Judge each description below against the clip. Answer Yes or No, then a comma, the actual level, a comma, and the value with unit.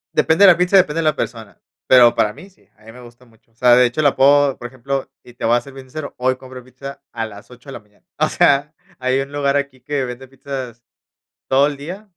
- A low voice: Yes, low, 130 Hz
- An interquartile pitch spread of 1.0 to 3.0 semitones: Yes, average, 2.7 semitones